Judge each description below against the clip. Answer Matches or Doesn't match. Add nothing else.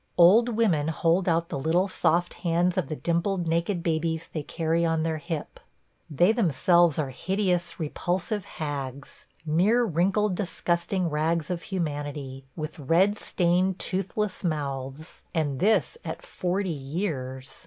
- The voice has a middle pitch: Matches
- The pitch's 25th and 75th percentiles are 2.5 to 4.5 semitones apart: Matches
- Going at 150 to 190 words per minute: Doesn't match